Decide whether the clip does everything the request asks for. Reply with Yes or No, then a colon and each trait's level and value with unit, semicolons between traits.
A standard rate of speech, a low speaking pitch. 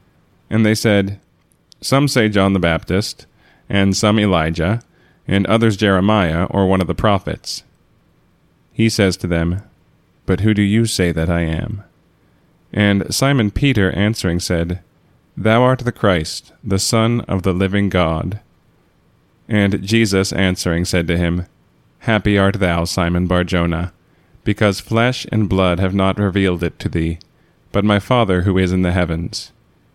Yes: average, 150 wpm; very low, 95 Hz